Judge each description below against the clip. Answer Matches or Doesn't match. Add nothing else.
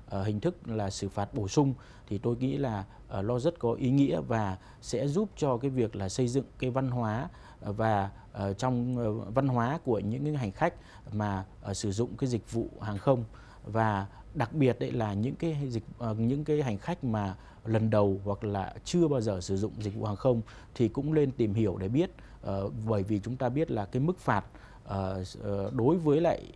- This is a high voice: Doesn't match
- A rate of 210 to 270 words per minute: Doesn't match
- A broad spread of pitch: Doesn't match